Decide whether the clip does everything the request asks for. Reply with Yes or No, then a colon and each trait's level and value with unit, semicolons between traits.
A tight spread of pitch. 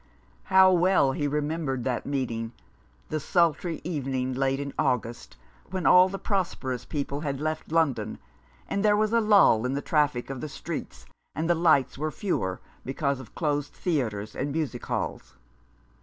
No: average, 4.4 semitones